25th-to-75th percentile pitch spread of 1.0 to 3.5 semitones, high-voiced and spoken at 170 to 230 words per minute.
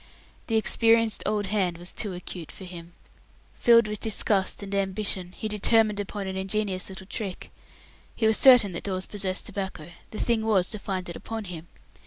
Yes: narrow, 2.6 semitones; high, 200 Hz; average, 180 wpm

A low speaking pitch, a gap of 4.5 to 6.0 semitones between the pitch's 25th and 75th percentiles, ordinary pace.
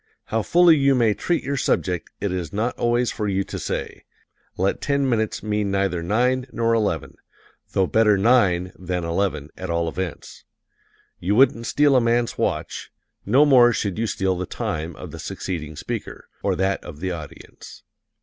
Yes: low, 105 Hz; average, 4.8 semitones; average, 175 wpm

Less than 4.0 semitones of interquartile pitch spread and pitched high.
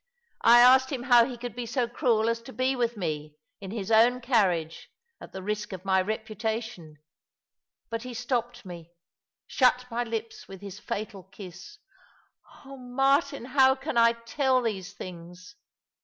No: average, 4.3 semitones; high, 230 Hz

